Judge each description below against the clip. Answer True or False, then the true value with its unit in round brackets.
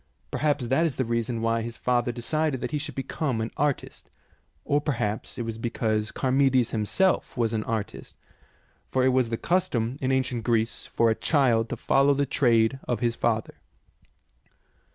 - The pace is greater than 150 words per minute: True (175 wpm)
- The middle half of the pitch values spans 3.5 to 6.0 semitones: False (3.1 semitones)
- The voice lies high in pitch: False (120 Hz)